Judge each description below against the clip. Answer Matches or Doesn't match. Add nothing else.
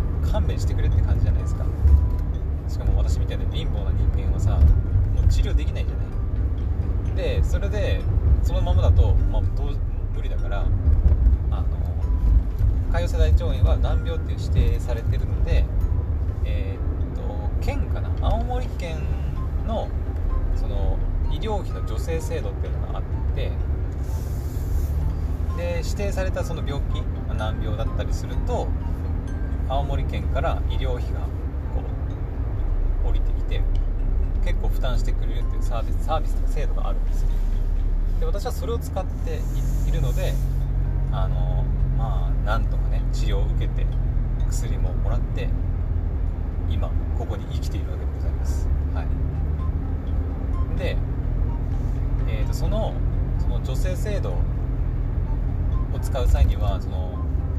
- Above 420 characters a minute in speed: Doesn't match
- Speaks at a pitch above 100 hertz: Doesn't match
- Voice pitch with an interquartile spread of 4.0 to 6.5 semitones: Doesn't match